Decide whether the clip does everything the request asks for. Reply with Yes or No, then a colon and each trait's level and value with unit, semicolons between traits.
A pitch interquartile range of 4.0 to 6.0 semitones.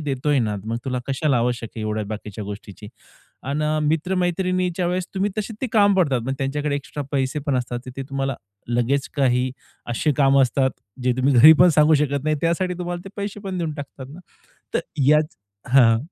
Yes: average, 5.1 semitones